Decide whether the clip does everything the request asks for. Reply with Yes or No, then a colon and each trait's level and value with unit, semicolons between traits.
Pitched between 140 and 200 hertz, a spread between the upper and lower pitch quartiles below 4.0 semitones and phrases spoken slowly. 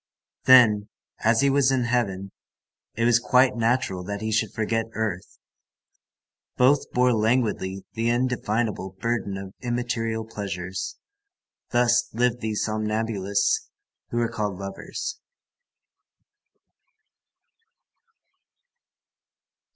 No: low, 115 Hz; average, 3.0 semitones; slow, 95 wpm